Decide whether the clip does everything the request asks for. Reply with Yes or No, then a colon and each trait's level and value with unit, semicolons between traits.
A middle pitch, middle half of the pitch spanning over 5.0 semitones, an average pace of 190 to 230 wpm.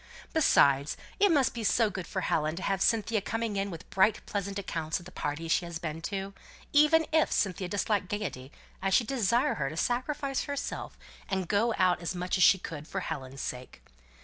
No: high, 195 Hz; wide, 5.4 semitones; average, 200 wpm